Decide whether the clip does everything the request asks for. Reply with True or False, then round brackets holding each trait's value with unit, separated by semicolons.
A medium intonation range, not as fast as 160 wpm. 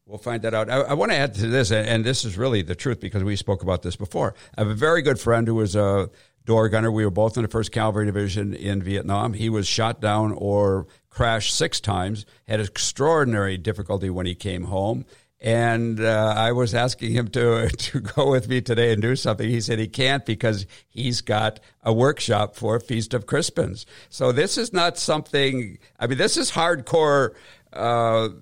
False (3.0 semitones; 205 wpm)